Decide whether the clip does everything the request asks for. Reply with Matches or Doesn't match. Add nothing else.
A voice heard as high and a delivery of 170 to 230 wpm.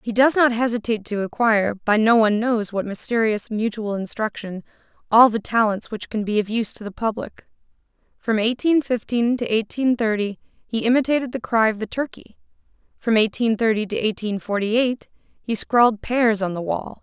Matches